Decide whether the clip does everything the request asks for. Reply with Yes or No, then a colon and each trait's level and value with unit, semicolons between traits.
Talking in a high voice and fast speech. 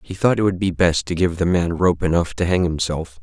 No: very low, 90 Hz; fast, 280 wpm